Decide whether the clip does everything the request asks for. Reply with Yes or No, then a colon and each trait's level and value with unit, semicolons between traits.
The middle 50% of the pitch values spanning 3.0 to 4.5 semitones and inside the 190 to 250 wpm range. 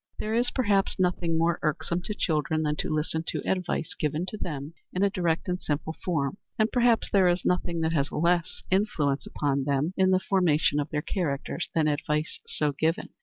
Yes: average, 3.7 semitones; average, 195 wpm